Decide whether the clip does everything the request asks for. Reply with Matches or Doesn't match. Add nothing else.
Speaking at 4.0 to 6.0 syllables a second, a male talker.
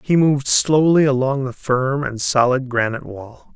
Matches